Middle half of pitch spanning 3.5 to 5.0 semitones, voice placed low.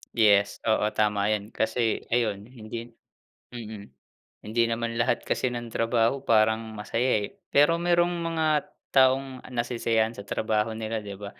No: average, 2.8 semitones; low, 115 Hz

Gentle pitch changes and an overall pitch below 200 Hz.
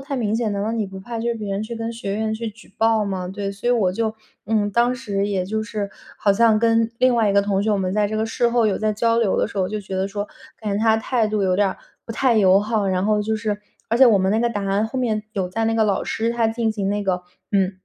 No: narrow, 2.2 semitones; high, 215 Hz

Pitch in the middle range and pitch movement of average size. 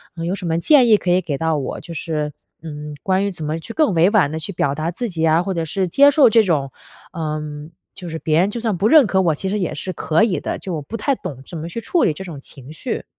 Yes: medium, 170 Hz; average, 4.4 semitones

